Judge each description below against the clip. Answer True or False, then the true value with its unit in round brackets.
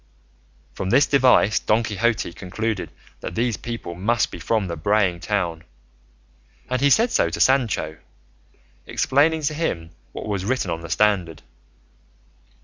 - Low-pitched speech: True (105 Hz)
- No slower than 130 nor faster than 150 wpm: True (140 wpm)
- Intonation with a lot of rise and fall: True (5.9 semitones)